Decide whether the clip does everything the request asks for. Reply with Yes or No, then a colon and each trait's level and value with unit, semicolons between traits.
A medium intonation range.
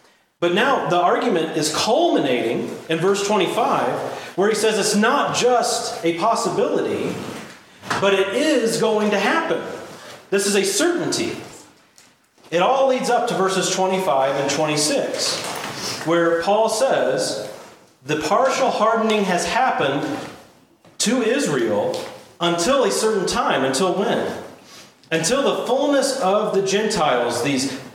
No: wide, 5.8 semitones